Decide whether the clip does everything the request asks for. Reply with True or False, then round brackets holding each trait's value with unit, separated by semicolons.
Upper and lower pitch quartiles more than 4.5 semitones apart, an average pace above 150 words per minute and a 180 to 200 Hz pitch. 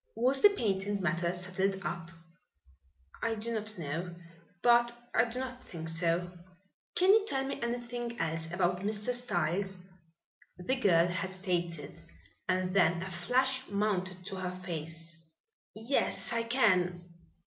False (5.2 semitones; 135 wpm; 190 Hz)